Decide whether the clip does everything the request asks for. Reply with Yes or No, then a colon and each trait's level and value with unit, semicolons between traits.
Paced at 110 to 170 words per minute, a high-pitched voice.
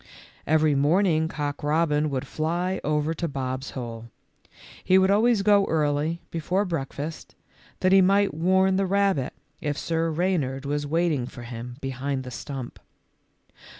No: average, 150 wpm; medium, 155 Hz